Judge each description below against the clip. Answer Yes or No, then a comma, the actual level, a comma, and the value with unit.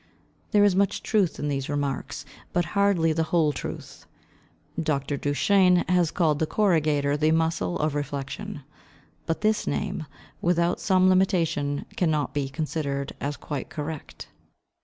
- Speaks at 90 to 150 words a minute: Yes, average, 140 wpm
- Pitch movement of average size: Yes, average, 3.9 semitones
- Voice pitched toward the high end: No, medium, 160 Hz